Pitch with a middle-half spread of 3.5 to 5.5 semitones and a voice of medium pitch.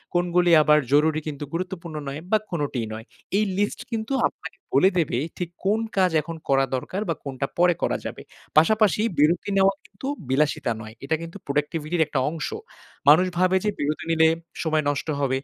Yes: average, 3.9 semitones; medium, 165 Hz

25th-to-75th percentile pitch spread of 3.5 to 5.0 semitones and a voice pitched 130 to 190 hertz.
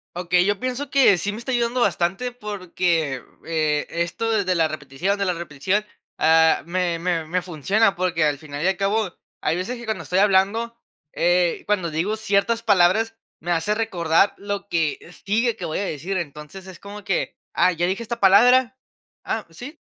Yes: average, 4.1 semitones; medium, 185 Hz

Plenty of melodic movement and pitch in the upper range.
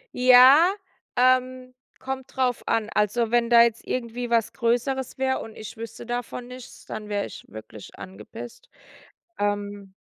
No: average, 2.9 semitones; high, 235 Hz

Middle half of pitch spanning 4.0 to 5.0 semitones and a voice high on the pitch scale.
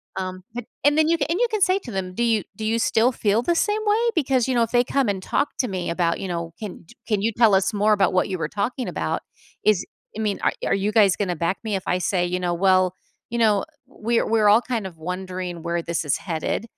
Yes: average, 4.5 semitones; high, 205 Hz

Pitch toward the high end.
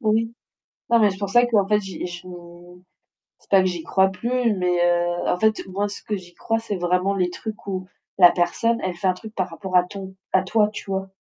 Yes: high, 195 Hz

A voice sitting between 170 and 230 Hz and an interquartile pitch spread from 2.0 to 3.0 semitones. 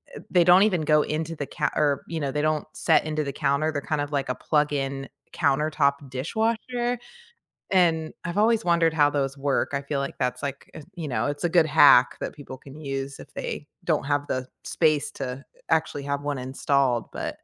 No: medium, 145 Hz; narrow, 2.6 semitones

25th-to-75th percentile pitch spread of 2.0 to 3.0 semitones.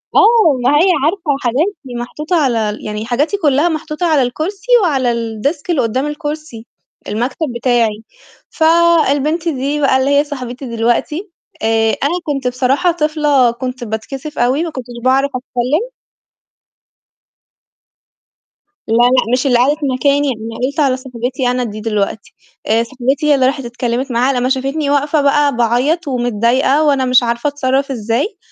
No: average, 3.7 semitones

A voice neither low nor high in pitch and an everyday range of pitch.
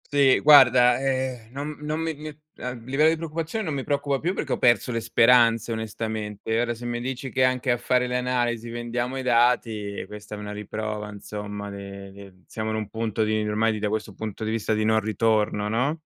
No: low, 115 Hz; average, 3.2 semitones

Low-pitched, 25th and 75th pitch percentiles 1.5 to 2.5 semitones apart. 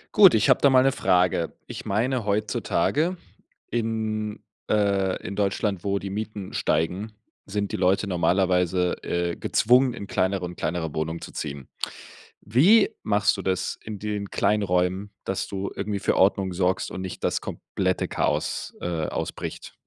No: low, 100 Hz; average, 2.9 semitones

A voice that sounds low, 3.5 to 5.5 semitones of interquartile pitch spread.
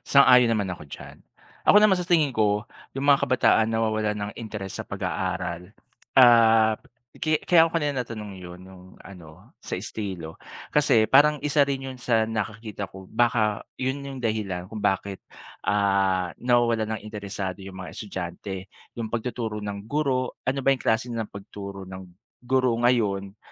Yes: low, 110 Hz; average, 4.3 semitones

